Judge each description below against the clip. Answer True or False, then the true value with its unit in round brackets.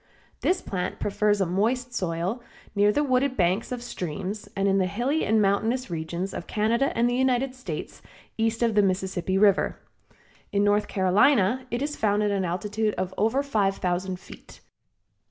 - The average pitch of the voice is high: True (205 Hz)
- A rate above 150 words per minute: True (170 wpm)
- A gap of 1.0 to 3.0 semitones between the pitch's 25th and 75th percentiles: False (4.2 semitones)